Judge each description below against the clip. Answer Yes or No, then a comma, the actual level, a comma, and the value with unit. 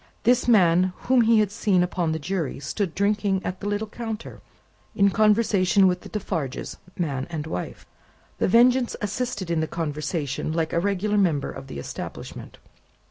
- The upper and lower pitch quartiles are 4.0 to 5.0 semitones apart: Yes, average, 4.4 semitones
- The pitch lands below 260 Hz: Yes, high, 190 Hz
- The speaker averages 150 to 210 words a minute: Yes, average, 165 wpm